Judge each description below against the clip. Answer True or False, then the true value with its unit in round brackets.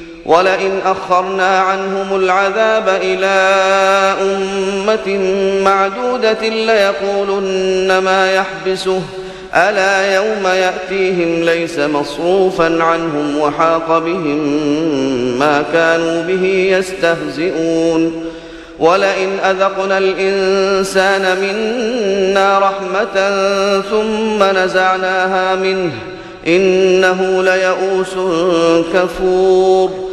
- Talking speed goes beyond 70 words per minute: False (65 wpm)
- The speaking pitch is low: False (190 Hz)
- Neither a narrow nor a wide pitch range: False (1.4 semitones)